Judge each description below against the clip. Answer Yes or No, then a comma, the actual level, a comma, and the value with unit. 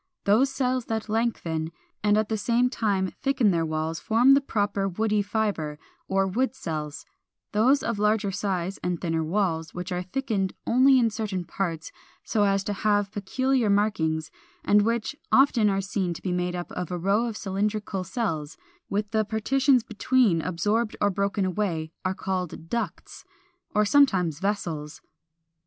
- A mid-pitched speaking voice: No, high, 205 Hz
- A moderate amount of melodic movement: Yes, average, 3.8 semitones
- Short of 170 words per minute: Yes, average, 160 wpm